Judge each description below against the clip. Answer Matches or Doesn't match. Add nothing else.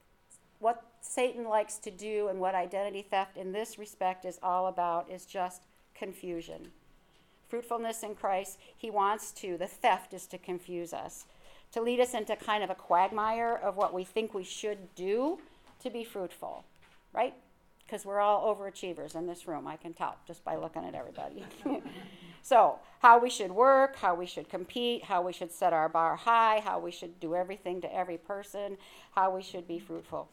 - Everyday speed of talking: Matches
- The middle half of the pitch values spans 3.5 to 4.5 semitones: Doesn't match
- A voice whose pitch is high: Matches